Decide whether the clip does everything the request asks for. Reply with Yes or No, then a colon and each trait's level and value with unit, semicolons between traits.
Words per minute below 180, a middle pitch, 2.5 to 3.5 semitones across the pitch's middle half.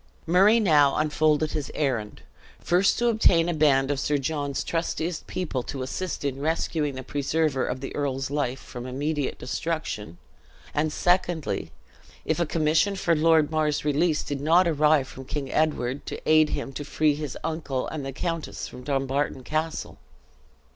Yes: average, 160 wpm; medium, 150 Hz; average, 3.0 semitones